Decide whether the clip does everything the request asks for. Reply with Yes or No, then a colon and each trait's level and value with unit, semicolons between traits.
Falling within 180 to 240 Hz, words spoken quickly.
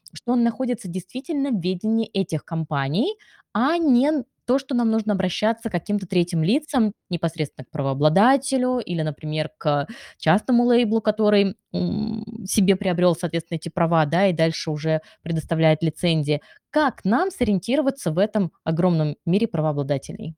No: high, 190 Hz; average, 140 wpm